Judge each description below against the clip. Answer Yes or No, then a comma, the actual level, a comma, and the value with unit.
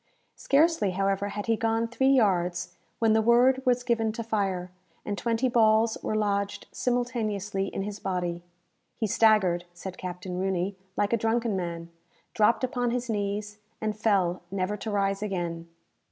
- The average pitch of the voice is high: Yes, high, 210 Hz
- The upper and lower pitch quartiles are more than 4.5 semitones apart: No, average, 3.2 semitones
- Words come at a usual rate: Yes, average, 155 wpm